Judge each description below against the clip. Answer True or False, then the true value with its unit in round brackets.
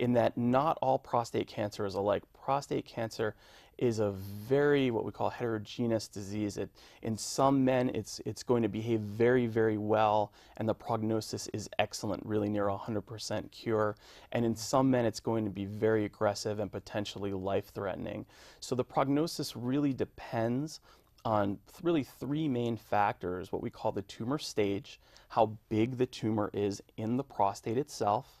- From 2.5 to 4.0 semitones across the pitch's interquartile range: True (3.1 semitones)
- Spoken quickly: False (165 wpm)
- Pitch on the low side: True (110 Hz)